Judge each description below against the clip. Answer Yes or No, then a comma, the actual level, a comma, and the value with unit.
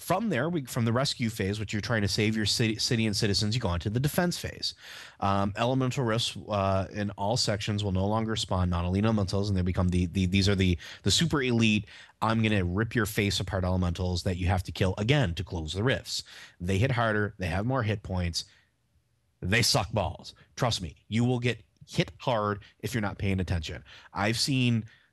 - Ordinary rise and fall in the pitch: Yes, average, 3.4 semitones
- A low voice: Yes, low, 105 Hz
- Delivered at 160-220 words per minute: Yes, fast, 205 wpm